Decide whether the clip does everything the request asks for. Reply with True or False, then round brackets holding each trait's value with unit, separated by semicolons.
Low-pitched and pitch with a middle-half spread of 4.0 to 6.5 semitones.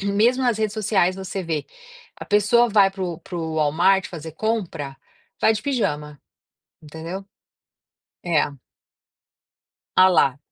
False (190 Hz; 4.8 semitones)